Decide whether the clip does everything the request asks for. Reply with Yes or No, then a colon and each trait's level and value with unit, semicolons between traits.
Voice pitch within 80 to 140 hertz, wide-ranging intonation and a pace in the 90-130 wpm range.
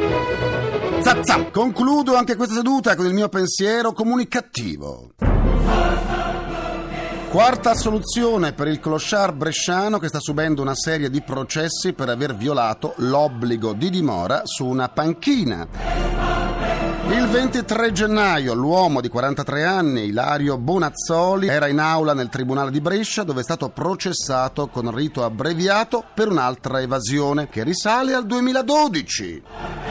No: medium, 160 Hz; wide, 7.6 semitones; average, 120 wpm